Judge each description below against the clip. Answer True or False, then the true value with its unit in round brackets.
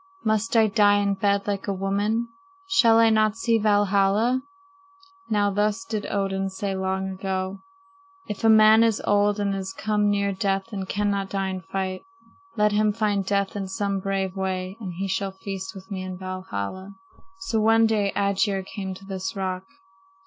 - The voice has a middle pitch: False (200 Hz)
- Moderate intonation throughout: False (1.6 semitones)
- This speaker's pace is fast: False (175 wpm)